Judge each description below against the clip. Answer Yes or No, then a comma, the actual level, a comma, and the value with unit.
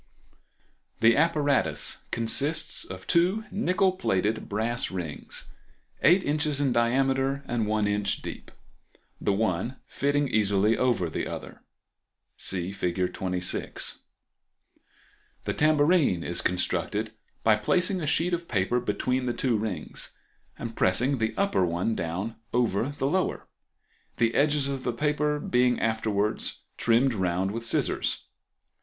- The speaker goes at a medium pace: No, slow, 125 wpm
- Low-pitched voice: Yes, low, 115 Hz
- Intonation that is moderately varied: No, wide, 6.1 semitones